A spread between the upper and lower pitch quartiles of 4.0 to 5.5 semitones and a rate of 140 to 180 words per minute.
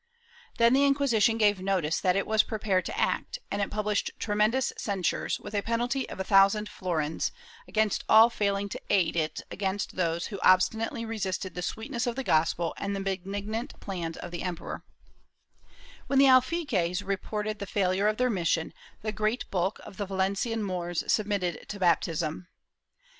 No: average, 3.1 semitones; average, 170 wpm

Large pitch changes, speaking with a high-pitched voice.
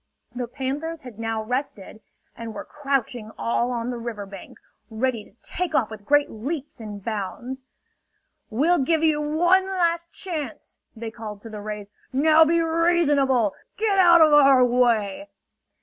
Yes: wide, 6.1 semitones; very high, 260 Hz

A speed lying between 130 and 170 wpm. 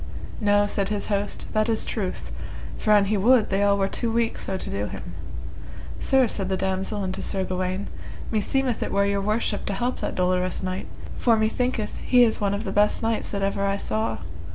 No: fast, 205 wpm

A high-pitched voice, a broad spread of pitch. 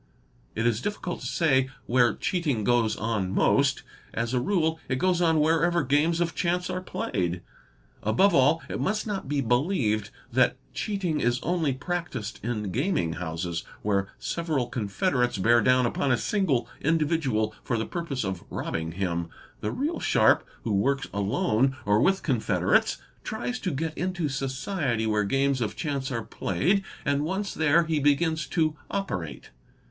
No: low, 135 Hz; wide, 7.2 semitones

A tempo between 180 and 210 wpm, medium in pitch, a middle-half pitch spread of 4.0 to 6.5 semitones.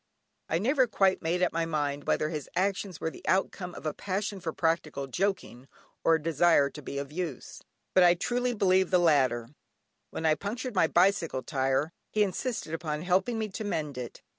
Yes: average, 195 wpm; medium, 170 Hz; average, 4.3 semitones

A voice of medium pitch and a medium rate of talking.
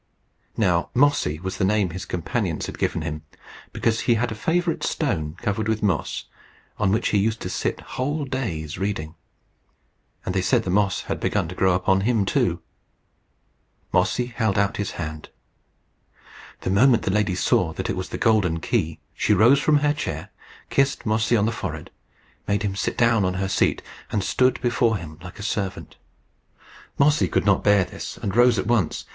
No: low, 105 Hz; average, 185 wpm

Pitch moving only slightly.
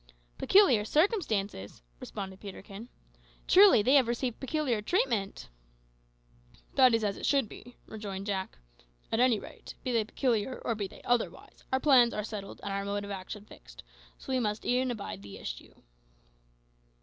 No: average, 4.3 semitones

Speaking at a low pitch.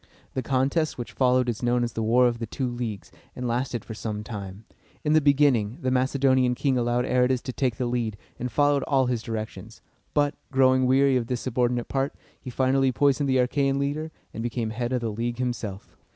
Yes: low, 125 Hz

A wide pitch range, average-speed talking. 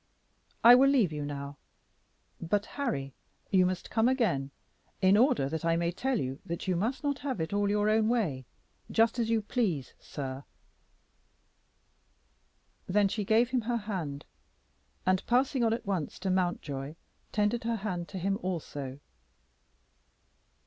Yes: wide, 6.1 semitones; average, 150 wpm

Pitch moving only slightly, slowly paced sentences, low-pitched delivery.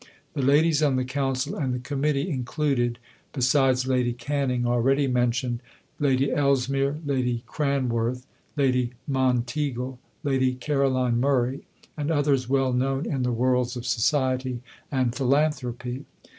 Yes: narrow, 2.0 semitones; slow, 125 wpm; low, 130 Hz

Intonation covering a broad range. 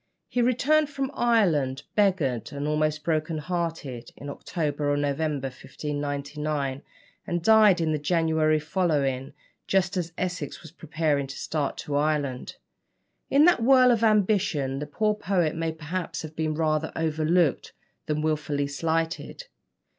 No: average, 3.8 semitones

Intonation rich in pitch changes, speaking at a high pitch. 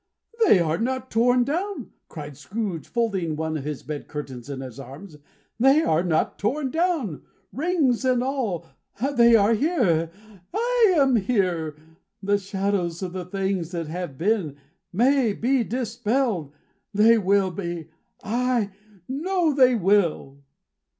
Yes: wide, 7.3 semitones; high, 205 Hz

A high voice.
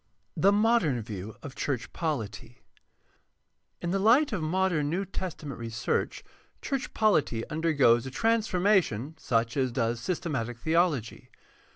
No: medium, 150 Hz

